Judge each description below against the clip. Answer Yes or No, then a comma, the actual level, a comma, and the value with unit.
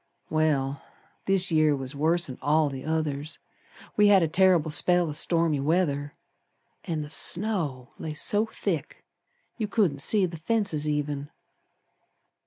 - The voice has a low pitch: No, medium, 155 Hz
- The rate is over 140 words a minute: No, slow, 135 wpm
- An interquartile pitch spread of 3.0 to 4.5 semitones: Yes, average, 3.8 semitones